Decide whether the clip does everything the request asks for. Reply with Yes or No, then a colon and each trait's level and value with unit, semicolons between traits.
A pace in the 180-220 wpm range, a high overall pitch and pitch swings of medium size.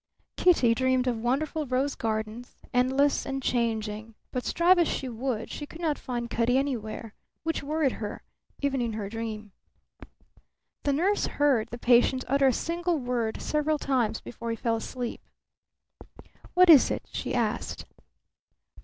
No: average, 150 wpm; very high, 250 Hz; average, 3.8 semitones